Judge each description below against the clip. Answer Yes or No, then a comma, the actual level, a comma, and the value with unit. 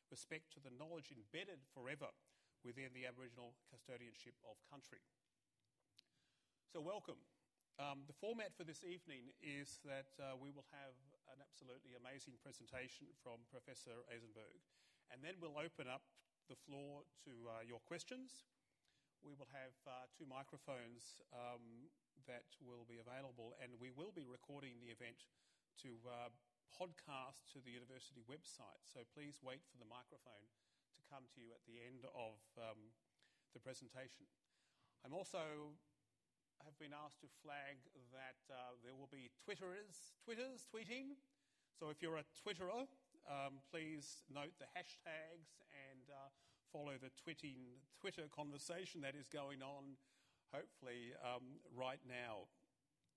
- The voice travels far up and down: No, average, 3.5 semitones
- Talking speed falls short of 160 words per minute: Yes, average, 140 wpm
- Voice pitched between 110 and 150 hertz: Yes, low, 135 Hz